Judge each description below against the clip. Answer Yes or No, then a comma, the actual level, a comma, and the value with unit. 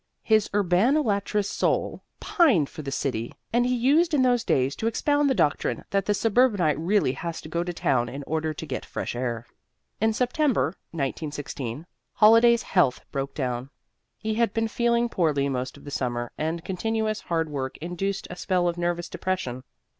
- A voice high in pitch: No, medium, 175 Hz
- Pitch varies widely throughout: Yes, wide, 7.9 semitones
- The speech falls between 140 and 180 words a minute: Yes, average, 175 wpm